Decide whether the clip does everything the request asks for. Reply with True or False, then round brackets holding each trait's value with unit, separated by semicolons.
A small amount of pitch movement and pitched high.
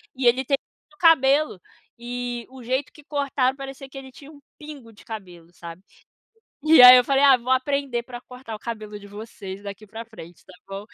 False (4.2 semitones; 250 Hz)